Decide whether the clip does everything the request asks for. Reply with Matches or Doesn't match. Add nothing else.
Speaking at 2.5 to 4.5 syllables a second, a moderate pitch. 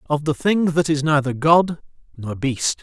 Matches